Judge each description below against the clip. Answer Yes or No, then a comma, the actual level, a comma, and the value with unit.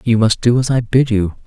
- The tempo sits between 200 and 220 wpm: No, fast, 285 wpm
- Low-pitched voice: Yes, low, 115 Hz